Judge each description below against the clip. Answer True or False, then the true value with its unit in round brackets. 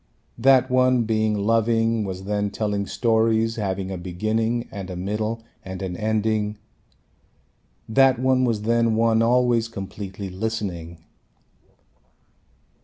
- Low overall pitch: True (110 Hz)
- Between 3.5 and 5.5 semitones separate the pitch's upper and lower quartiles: False (2.6 semitones)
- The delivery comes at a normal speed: False (115 wpm)